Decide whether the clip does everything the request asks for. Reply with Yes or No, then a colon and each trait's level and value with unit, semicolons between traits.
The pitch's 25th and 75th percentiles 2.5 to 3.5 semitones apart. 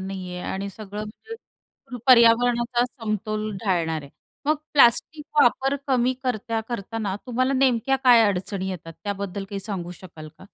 No: average, 4.3 semitones